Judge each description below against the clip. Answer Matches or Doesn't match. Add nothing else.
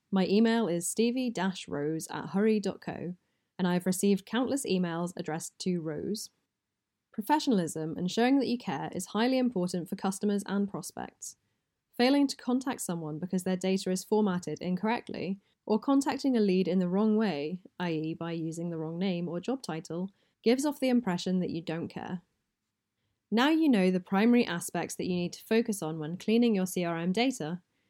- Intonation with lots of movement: Doesn't match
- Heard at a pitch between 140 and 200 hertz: Matches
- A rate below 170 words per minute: Doesn't match